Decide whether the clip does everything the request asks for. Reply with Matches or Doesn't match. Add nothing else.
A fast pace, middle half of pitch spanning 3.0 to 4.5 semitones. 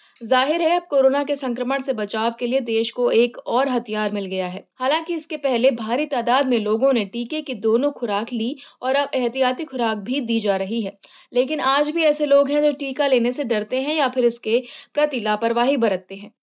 Matches